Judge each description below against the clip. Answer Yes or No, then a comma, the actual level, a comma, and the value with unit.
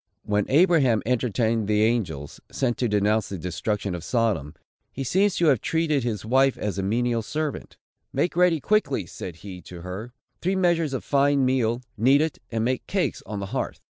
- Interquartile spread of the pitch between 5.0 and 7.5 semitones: Yes, wide, 5.4 semitones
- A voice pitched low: Yes, low, 120 Hz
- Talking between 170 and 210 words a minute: Yes, average, 185 wpm